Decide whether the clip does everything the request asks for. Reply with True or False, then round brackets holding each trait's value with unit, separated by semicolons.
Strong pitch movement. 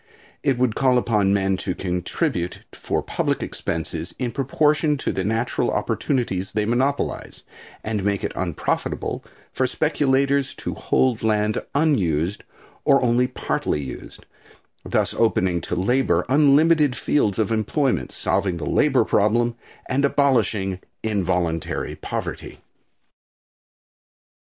True (6.0 semitones)